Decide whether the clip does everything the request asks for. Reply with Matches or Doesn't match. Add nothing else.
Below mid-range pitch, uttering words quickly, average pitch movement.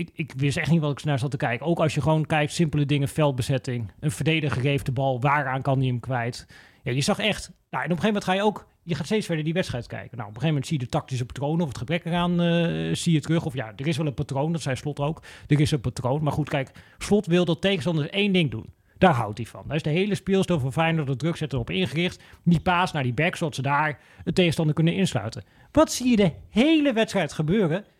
Doesn't match